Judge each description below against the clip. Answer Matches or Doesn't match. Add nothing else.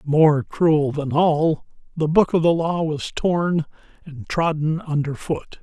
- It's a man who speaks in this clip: Matches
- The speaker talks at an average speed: Matches